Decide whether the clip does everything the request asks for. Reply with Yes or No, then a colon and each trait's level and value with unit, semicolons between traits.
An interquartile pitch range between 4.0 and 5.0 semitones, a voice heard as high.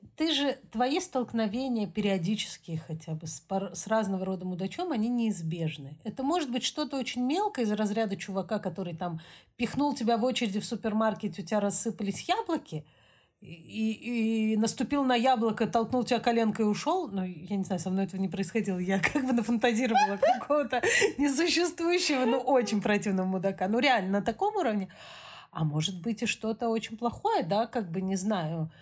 Yes: average, 4.7 semitones; high, 220 Hz